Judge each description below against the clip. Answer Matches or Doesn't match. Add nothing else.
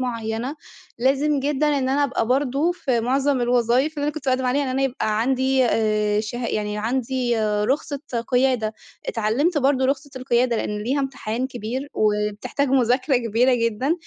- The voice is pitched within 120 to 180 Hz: Doesn't match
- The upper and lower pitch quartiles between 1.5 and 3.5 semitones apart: Matches